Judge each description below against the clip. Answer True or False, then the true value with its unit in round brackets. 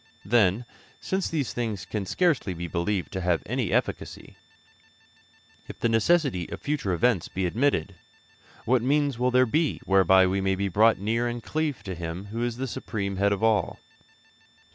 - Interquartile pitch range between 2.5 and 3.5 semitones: False (4.9 semitones)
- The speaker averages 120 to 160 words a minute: False (170 wpm)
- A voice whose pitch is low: True (110 Hz)